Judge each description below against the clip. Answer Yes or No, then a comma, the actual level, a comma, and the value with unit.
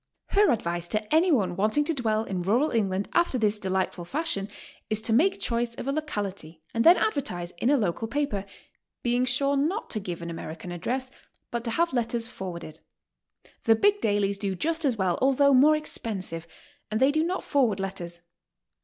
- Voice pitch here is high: Yes, high, 225 Hz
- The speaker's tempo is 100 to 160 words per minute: No, average, 180 wpm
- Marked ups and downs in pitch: Yes, wide, 6.7 semitones